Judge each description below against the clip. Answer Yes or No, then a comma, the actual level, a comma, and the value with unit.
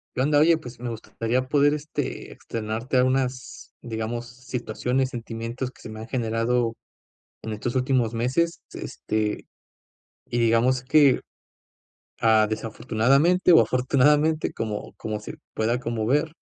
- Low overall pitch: Yes, low, 125 Hz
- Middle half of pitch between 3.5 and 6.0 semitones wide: No, average, 2.9 semitones